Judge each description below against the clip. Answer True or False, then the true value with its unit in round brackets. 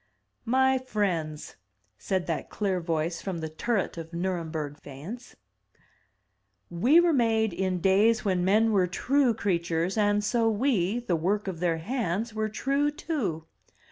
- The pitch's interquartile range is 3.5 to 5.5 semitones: True (5.1 semitones)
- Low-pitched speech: False (195 Hz)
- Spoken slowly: False (150 wpm)